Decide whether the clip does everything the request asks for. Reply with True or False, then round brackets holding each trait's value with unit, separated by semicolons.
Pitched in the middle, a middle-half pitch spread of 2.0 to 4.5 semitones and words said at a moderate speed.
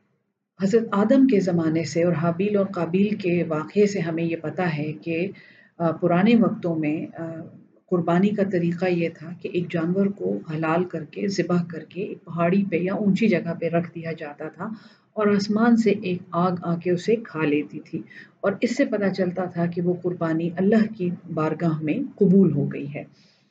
True (180 Hz; 3.1 semitones; 185 wpm)